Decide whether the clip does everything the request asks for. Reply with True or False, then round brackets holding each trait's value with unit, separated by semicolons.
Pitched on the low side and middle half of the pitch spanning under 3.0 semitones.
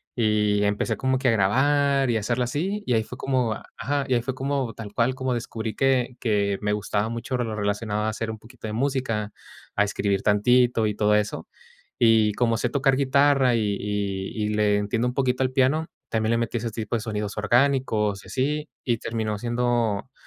False (115 Hz; 3.5 semitones)